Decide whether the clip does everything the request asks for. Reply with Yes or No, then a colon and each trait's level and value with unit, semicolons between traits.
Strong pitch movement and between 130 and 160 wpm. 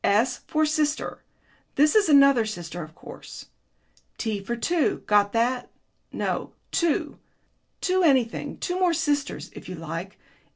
Yes: wide, 7.2 semitones; slow, 135 wpm